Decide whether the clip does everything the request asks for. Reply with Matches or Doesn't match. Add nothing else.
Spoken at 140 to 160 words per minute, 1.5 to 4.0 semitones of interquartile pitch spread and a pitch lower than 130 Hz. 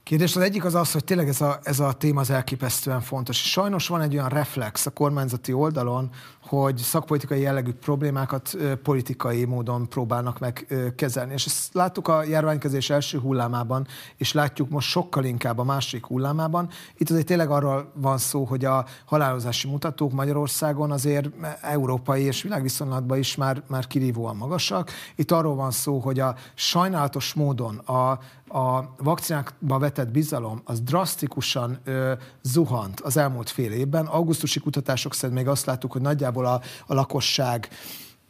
Doesn't match